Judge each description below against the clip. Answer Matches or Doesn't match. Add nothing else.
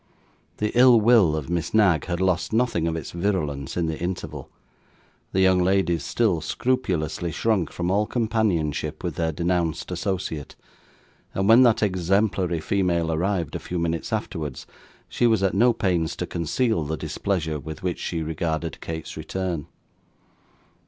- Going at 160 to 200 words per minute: Doesn't match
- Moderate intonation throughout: Matches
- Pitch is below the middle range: Matches